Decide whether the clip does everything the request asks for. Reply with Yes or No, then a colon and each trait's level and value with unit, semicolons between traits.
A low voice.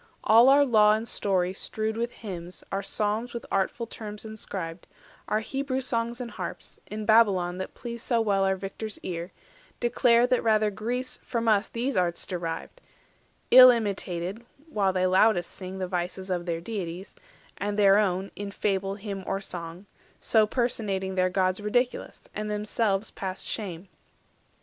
No: high, 205 Hz